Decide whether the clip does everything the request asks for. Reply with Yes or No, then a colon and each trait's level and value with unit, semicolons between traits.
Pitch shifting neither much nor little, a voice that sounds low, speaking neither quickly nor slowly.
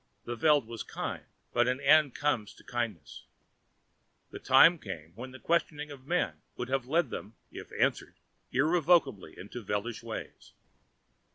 Yes: average, 4.5 semitones; low, 130 Hz; average, 150 wpm